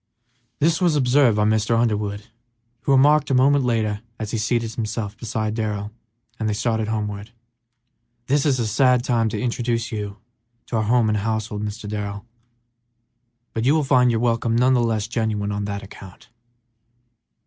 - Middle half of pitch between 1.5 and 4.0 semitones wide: Yes, average, 2.8 semitones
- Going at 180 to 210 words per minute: No, average, 170 wpm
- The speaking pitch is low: Yes, low, 110 Hz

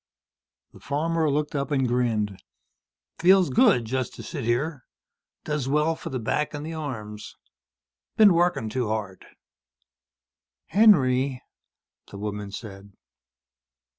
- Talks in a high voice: No, low, 135 Hz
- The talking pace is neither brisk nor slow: No, slow, 120 wpm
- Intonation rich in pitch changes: Yes, wide, 6.1 semitones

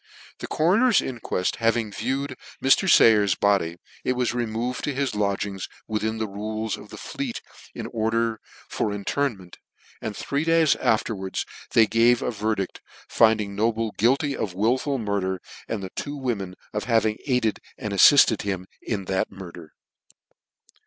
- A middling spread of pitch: Yes, average, 3.7 semitones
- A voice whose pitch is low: Yes, low, 110 Hz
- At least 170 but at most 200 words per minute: No, average, 150 wpm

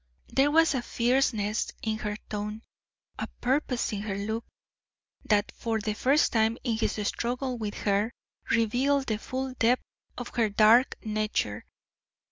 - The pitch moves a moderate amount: Yes, average, 3.0 semitones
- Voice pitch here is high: Yes, high, 225 Hz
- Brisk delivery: No, average, 145 wpm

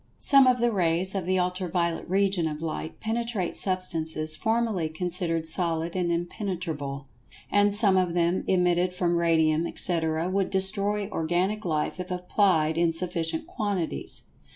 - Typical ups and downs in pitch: Yes, average, 3.0 semitones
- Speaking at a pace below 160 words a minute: Yes, average, 150 wpm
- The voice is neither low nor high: Yes, medium, 180 Hz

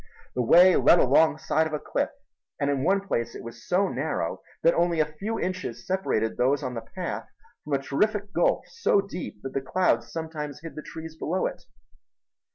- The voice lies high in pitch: No, medium, 160 Hz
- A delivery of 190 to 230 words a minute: Yes, average, 200 wpm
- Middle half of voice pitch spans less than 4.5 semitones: No, average, 5.0 semitones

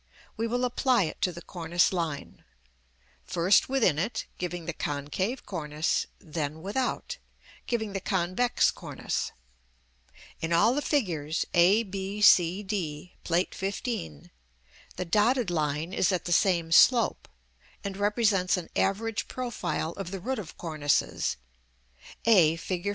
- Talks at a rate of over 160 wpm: No, slow, 135 wpm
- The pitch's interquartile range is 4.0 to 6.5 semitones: Yes, average, 4.4 semitones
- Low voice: No, medium, 185 Hz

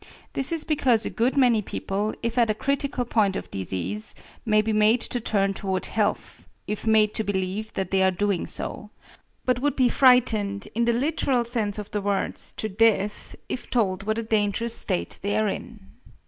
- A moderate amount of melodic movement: Yes, average, 3.0 semitones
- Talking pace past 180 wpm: Yes, average, 190 wpm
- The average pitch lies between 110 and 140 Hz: No, high, 215 Hz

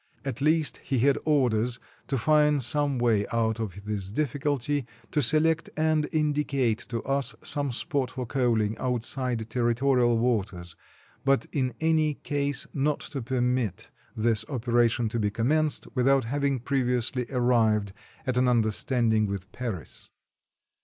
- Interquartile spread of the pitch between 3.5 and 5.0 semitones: Yes, average, 3.8 semitones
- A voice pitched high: No, low, 125 Hz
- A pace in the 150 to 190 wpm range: No, slow, 135 wpm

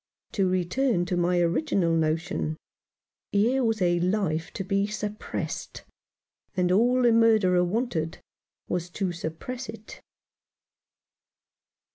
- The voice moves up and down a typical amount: Yes, average, 4.2 semitones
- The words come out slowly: Yes, slow, 110 wpm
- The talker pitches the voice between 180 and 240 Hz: Yes, medium, 185 Hz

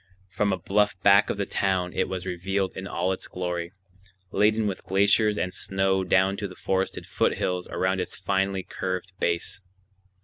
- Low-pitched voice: Yes, very low, 95 Hz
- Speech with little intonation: Yes, narrow, 1.4 semitones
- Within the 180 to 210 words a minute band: No, average, 170 wpm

